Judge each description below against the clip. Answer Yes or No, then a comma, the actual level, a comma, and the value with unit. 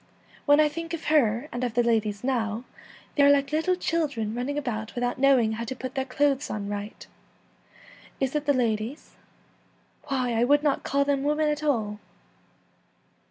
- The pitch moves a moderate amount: Yes, average, 4.2 semitones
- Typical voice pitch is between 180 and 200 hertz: No, very high, 265 Hz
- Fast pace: No, average, 185 wpm